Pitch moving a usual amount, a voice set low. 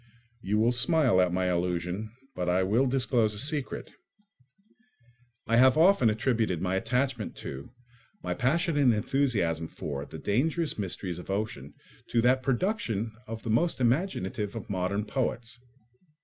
No: wide, 5.8 semitones; low, 115 Hz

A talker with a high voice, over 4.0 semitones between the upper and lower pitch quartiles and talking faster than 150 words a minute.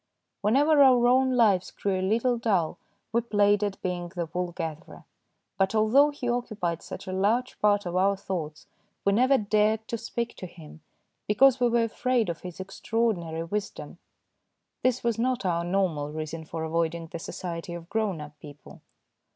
Yes: high, 200 Hz; wide, 5.4 semitones; average, 175 wpm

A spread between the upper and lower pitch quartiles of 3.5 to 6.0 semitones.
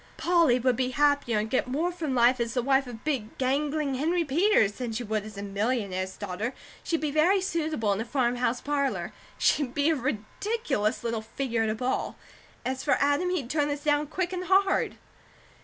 Yes: average, 4.9 semitones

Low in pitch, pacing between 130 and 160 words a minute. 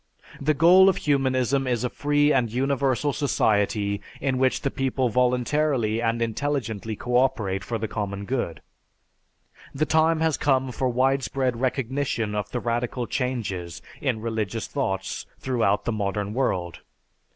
Yes: low, 125 Hz; average, 140 wpm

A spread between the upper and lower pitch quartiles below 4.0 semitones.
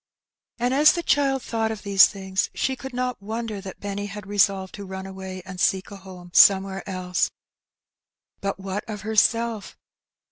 Yes: average, 2.9 semitones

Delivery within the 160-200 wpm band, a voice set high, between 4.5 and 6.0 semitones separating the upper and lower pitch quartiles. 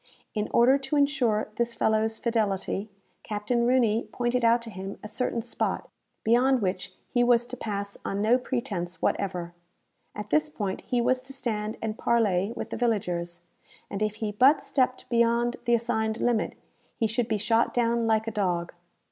No: average, 175 wpm; high, 225 Hz; narrow, 2.6 semitones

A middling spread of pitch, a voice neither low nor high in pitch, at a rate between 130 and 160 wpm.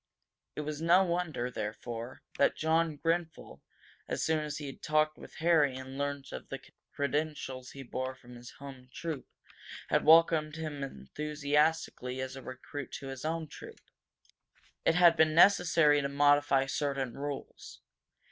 Yes: average, 3.1 semitones; medium, 145 Hz; average, 150 wpm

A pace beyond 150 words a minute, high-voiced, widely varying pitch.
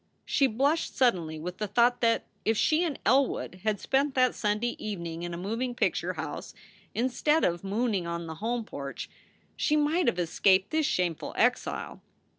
Yes: average, 170 wpm; high, 220 Hz; wide, 6.6 semitones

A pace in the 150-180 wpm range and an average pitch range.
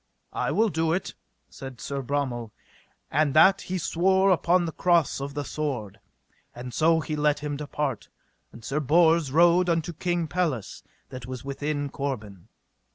Yes: average, 160 wpm; average, 4.0 semitones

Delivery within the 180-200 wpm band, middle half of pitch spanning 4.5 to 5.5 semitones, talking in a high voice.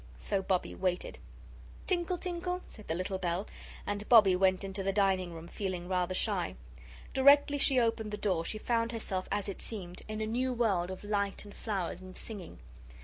No: average, 185 wpm; average, 3.6 semitones; high, 200 Hz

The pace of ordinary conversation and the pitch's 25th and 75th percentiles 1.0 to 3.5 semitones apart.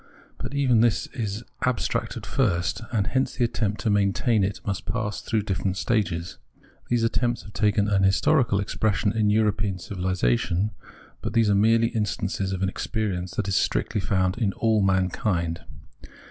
Yes: average, 160 wpm; average, 2.9 semitones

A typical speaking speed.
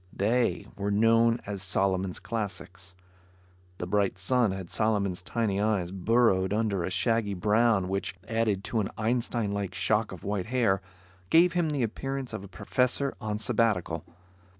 Yes: average, 150 wpm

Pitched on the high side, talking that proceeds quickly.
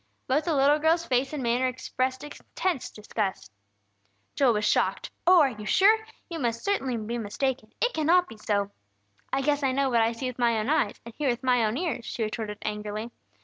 Yes: very high, 255 Hz; fast, 215 wpm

